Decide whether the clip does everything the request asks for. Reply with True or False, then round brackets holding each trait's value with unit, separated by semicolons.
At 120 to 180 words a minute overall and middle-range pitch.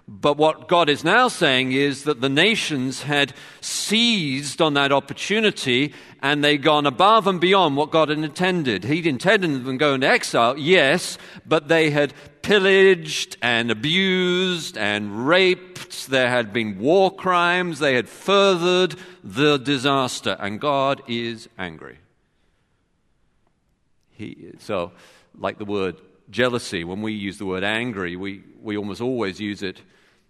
True (145 wpm; 145 Hz)